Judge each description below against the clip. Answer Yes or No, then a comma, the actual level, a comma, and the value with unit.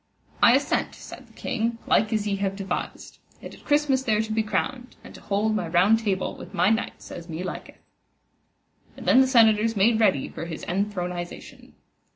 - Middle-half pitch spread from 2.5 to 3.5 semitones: Yes, average, 3.1 semitones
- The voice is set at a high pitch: Yes, high, 210 Hz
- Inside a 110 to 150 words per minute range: No, average, 190 wpm